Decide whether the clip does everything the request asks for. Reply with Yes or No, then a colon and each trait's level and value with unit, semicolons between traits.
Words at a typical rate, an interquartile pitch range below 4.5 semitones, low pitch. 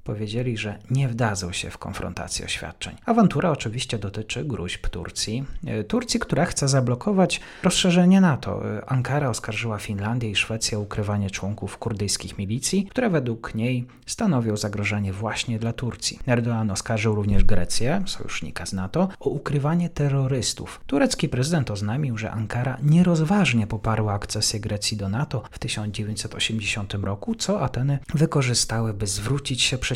No: average, 135 wpm; average, 5.2 semitones; low, 115 Hz